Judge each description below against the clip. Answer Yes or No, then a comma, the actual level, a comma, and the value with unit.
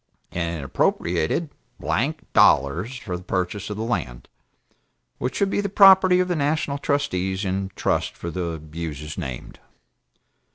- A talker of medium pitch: No, very low, 95 Hz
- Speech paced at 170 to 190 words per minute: No, average, 150 wpm